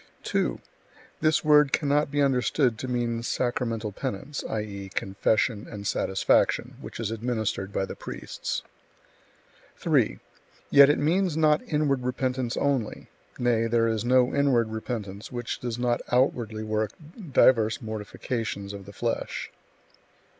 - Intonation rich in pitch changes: No, average, 3.6 semitones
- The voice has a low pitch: Yes, low, 120 Hz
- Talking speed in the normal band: No, slow, 130 wpm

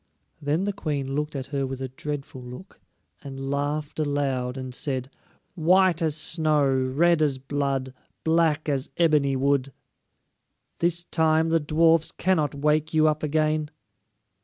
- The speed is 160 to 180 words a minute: No, average, 140 wpm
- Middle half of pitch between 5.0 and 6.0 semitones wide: No, average, 2.7 semitones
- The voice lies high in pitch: No, medium, 150 Hz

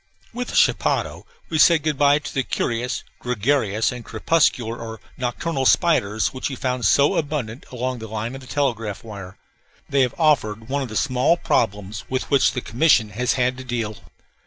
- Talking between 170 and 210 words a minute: Yes, average, 180 wpm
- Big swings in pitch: No, average, 4.0 semitones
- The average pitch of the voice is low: Yes, low, 125 Hz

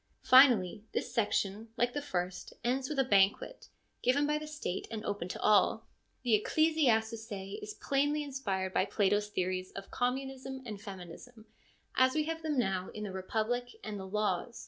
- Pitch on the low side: No, high, 225 Hz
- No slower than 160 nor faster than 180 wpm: Yes, average, 170 wpm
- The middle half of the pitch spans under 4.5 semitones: No, average, 5.3 semitones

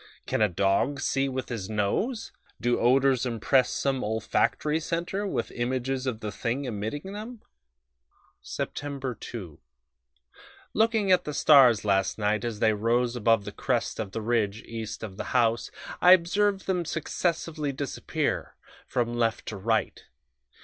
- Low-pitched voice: Yes, low, 125 Hz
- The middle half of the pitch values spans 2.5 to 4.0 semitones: No, average, 5.2 semitones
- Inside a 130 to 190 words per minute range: Yes, average, 145 wpm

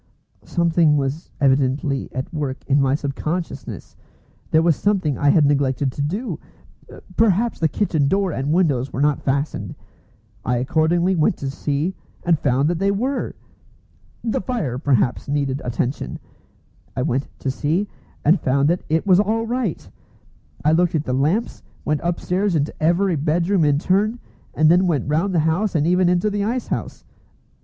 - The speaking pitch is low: No, medium, 160 Hz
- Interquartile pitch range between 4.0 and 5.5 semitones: Yes, average, 4.8 semitones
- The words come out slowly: No, average, 165 wpm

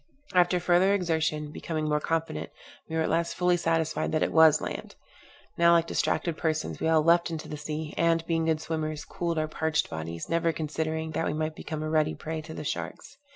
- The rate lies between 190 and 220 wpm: Yes, fast, 205 wpm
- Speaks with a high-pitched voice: No, medium, 160 Hz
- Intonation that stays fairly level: Yes, narrow, 1.3 semitones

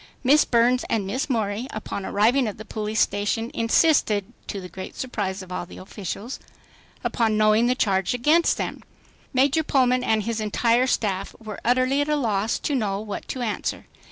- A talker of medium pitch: No, high, 225 Hz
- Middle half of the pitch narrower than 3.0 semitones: No, average, 3.8 semitones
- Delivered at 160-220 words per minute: Yes, average, 180 wpm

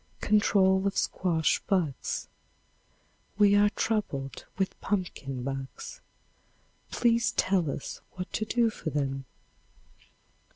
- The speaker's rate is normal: No, slow, 100 wpm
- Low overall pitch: No, high, 190 Hz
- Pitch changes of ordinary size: No, wide, 6.8 semitones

